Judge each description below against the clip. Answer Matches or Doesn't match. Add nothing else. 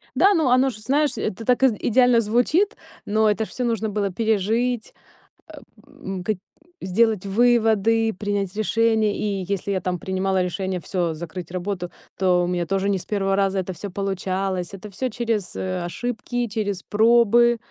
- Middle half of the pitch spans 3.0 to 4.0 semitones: Matches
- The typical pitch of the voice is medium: Doesn't match